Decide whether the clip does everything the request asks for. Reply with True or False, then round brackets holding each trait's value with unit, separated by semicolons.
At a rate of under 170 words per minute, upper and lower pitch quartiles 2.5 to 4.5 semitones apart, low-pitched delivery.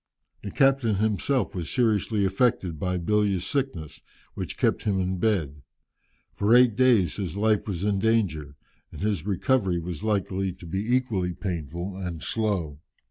True (150 wpm; 3.8 semitones; 100 Hz)